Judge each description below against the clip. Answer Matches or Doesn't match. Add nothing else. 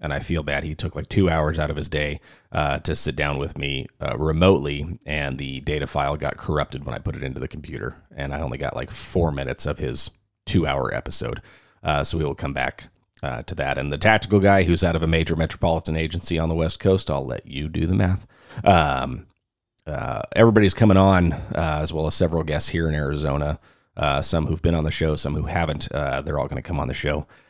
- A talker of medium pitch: Doesn't match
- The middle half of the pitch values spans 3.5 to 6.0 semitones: Doesn't match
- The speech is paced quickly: Matches